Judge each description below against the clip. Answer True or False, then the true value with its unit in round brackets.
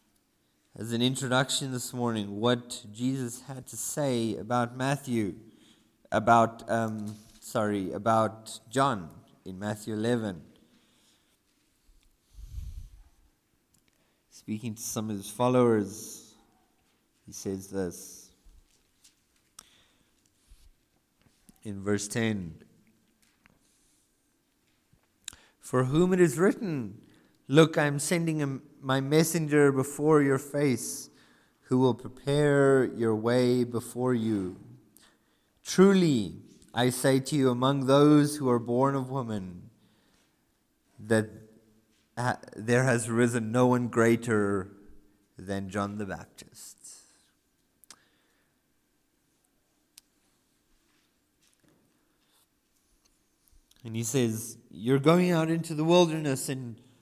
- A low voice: True (120 Hz)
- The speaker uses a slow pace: True (95 wpm)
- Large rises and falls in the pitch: False (4.1 semitones)